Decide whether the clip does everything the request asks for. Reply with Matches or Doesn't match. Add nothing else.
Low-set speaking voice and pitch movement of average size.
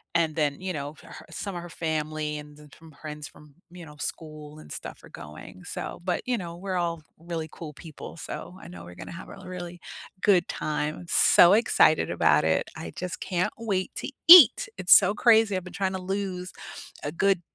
Doesn't match